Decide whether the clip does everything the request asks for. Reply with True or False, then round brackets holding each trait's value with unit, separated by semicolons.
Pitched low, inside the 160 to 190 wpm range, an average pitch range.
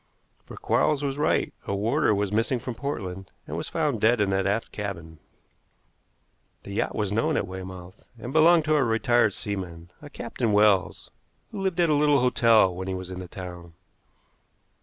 False (105 Hz; 180 wpm; 6.2 semitones)